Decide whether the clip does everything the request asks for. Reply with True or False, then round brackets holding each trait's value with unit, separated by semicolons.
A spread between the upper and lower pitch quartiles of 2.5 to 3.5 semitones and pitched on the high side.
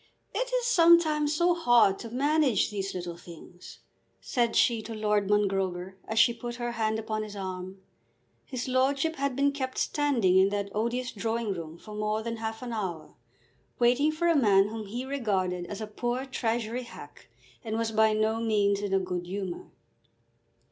False (4.3 semitones; 220 Hz)